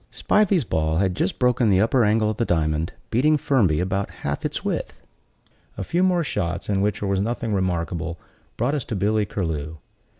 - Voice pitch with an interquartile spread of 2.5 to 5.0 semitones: No, wide, 5.6 semitones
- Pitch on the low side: Yes, low, 100 Hz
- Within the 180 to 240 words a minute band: Yes, average, 190 wpm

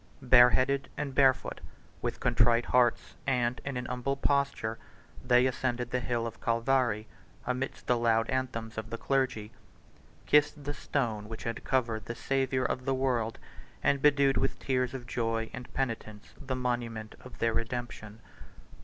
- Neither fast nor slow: Yes, average, 155 wpm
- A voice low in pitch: Yes, low, 125 Hz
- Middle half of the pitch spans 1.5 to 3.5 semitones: Yes, narrow, 2.4 semitones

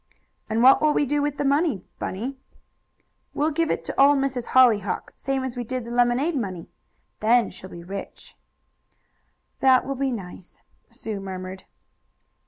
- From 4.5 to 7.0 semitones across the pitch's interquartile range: Yes, average, 5.1 semitones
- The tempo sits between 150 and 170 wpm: Yes, average, 165 wpm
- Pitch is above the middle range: Yes, very high, 250 Hz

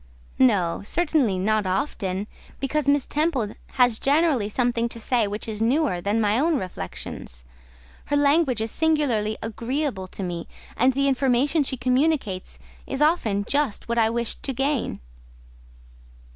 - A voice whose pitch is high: Yes, high, 245 Hz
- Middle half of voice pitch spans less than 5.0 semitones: No, average, 5.3 semitones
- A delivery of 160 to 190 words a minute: No, average, 145 wpm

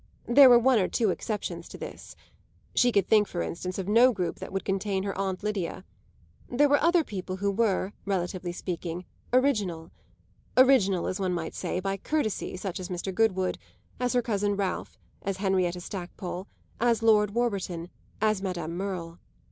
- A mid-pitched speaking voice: No, high, 195 Hz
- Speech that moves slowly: No, average, 170 wpm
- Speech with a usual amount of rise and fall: Yes, average, 3.4 semitones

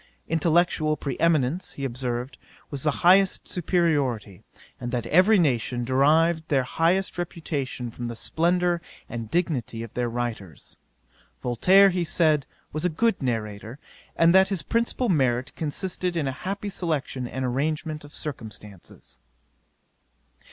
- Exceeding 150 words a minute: No, slow, 135 wpm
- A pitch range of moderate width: No, wide, 6.0 semitones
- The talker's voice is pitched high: No, medium, 150 Hz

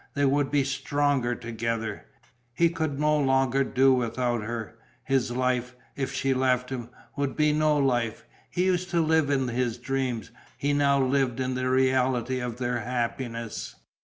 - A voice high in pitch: No, low, 130 Hz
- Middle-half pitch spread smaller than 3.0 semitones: Yes, narrow, 2.6 semitones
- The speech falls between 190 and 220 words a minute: No, average, 160 wpm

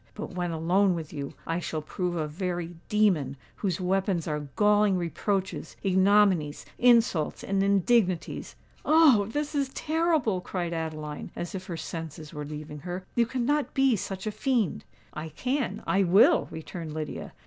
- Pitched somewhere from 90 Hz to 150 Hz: No, medium, 185 Hz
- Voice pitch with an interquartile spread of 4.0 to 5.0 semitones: Yes, average, 4.6 semitones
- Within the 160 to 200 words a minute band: No, average, 150 wpm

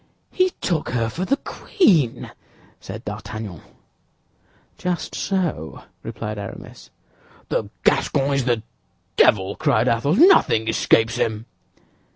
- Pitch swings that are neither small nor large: No, wide, 7.8 semitones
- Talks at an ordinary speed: No, slow, 110 wpm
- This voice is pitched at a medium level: No, low, 115 Hz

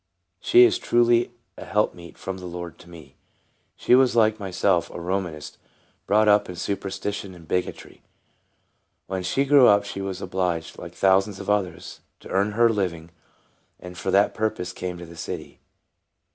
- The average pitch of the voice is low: Yes, very low, 95 Hz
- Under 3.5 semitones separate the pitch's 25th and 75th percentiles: Yes, average, 2.9 semitones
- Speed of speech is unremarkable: Yes, average, 170 wpm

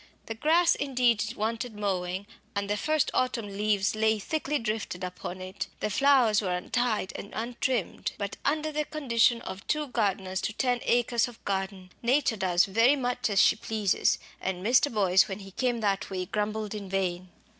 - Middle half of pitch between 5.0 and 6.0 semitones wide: No, average, 4.2 semitones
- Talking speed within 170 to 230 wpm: Yes, average, 175 wpm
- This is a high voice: Yes, high, 215 Hz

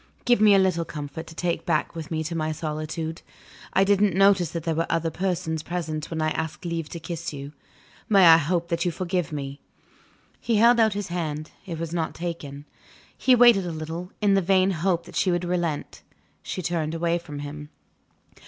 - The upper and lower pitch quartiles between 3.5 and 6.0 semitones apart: No, average, 2.7 semitones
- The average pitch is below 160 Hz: No, medium, 170 Hz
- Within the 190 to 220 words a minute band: Yes, average, 200 wpm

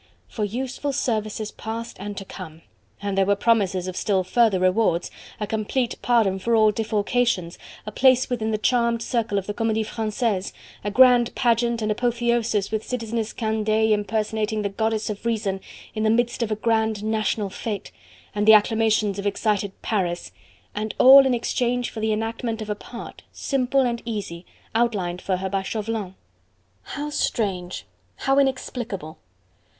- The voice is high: Yes, high, 220 Hz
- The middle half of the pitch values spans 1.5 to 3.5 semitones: Yes, narrow, 2.5 semitones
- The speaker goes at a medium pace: Yes, average, 160 wpm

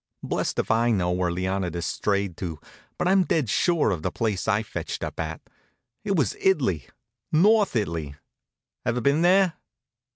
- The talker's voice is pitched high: No, low, 110 Hz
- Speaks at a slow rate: No, average, 160 wpm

